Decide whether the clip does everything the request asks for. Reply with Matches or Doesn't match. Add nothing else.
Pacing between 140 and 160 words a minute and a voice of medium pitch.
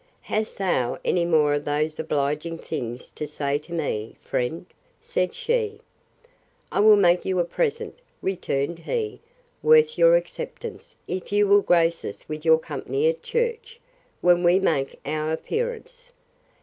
Matches